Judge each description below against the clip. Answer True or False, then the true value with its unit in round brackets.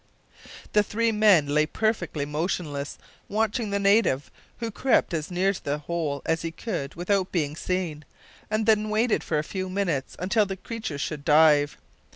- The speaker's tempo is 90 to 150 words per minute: False (170 wpm)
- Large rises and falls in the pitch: True (5.8 semitones)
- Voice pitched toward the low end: False (180 Hz)